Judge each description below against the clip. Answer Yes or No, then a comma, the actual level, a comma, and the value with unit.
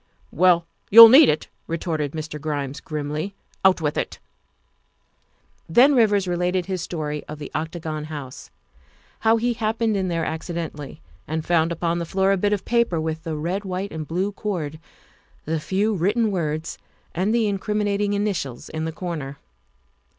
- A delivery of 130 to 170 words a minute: Yes, average, 165 wpm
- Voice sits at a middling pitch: Yes, medium, 175 Hz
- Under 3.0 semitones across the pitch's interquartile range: No, average, 4.4 semitones